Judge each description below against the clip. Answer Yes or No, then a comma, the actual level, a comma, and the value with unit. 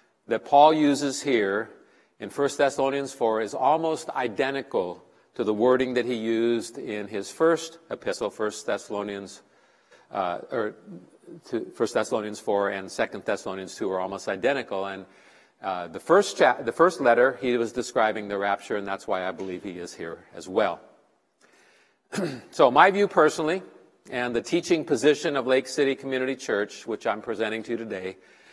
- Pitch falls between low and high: No, low, 120 Hz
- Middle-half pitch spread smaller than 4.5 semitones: No, wide, 5.6 semitones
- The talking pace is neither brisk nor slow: Yes, average, 165 wpm